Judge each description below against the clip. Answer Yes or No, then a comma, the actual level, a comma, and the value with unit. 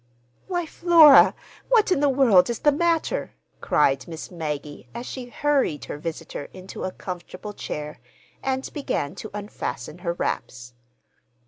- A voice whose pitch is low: No, high, 205 Hz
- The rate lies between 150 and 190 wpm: No, average, 140 wpm